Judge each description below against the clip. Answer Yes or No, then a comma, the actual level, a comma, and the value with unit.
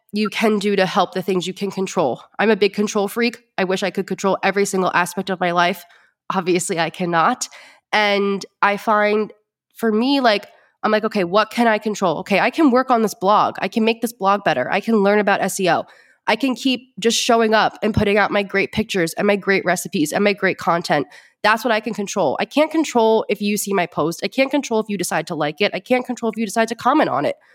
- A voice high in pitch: Yes, high, 205 Hz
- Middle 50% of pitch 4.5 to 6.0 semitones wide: No, average, 3.0 semitones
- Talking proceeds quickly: Yes, fast, 245 wpm